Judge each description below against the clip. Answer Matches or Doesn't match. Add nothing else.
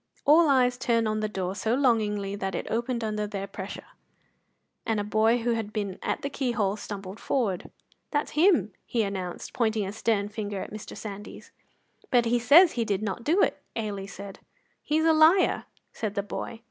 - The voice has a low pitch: Doesn't match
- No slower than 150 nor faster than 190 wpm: Matches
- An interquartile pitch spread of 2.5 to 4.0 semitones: Matches